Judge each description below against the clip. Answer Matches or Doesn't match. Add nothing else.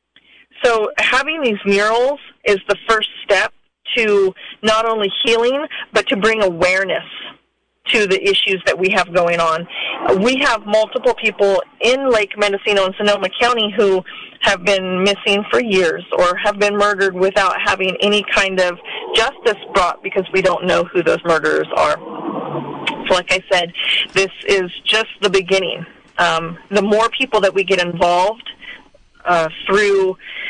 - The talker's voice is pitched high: Matches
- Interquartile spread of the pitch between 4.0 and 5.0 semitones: Doesn't match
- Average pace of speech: Matches